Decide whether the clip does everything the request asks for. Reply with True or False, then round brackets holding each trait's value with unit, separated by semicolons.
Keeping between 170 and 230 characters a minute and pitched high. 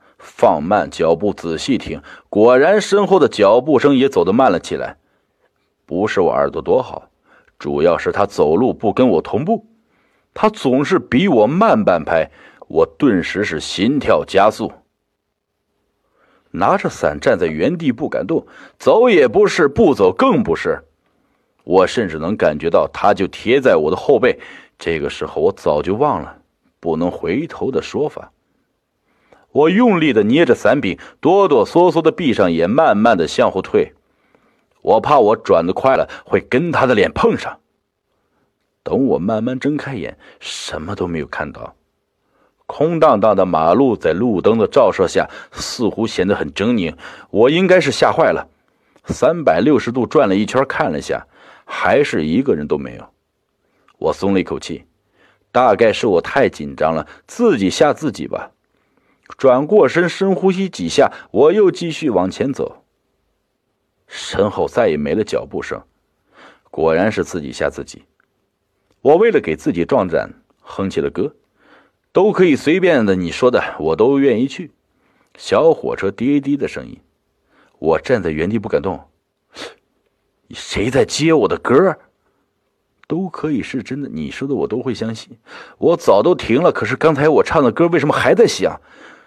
True (225 characters per minute; 260 Hz)